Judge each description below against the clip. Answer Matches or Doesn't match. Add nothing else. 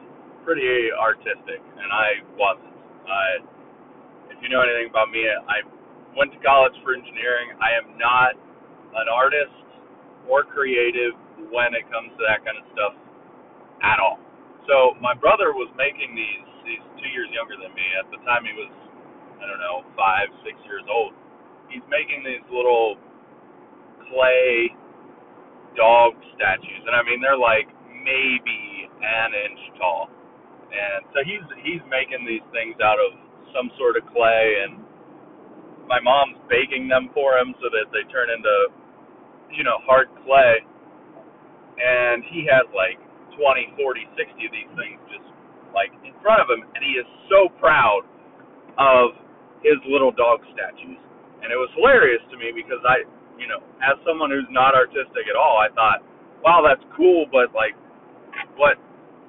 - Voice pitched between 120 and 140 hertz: Matches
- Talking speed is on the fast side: Doesn't match